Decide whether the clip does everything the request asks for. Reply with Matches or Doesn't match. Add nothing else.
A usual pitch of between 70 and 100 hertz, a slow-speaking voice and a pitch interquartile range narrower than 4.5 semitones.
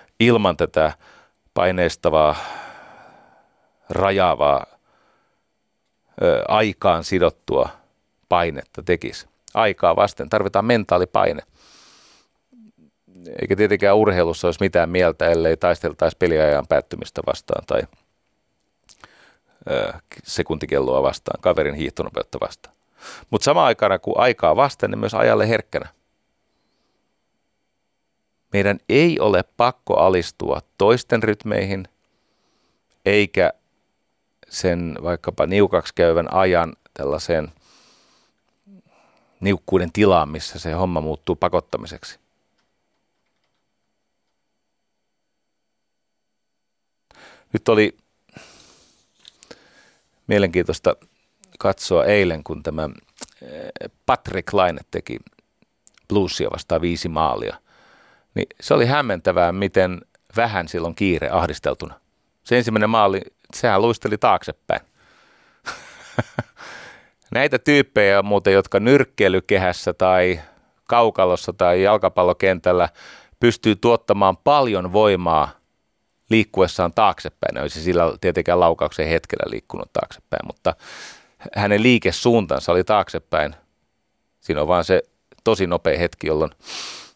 Matches